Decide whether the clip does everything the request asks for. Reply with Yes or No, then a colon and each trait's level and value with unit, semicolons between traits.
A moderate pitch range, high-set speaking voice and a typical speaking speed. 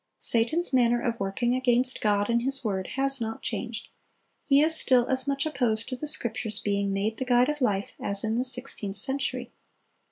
Yes: average, 3.3 semitones; high, 240 Hz; average, 190 wpm